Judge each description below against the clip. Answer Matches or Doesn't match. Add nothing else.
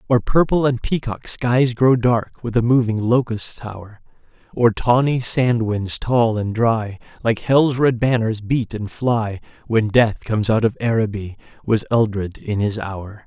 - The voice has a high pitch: Doesn't match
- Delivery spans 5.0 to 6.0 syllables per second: Doesn't match